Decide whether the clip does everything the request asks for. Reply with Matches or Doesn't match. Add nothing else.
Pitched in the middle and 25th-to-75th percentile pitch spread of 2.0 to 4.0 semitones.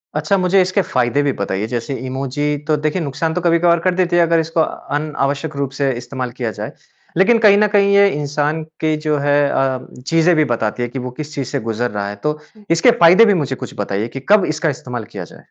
Doesn't match